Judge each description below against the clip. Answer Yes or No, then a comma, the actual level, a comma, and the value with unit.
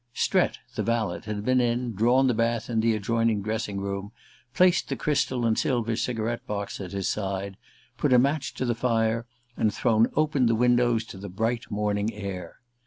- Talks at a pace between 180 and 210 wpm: Yes, average, 185 wpm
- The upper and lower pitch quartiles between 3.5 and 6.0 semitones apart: No, average, 2.9 semitones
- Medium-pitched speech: No, low, 115 Hz